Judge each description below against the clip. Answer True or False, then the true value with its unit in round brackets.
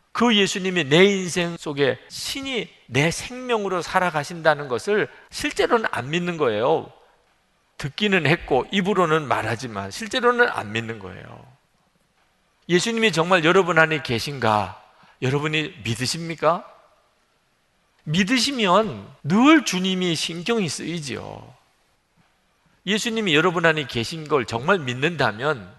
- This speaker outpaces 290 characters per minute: False (265 characters per minute)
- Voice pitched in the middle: True (170 Hz)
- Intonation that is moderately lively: False (6.0 semitones)